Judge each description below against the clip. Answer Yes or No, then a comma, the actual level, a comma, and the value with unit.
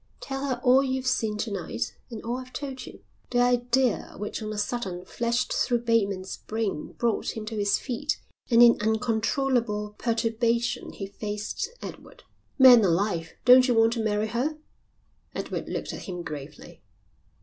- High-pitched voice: Yes, high, 230 Hz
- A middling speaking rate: Yes, average, 160 wpm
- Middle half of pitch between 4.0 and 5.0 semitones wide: No, average, 3.0 semitones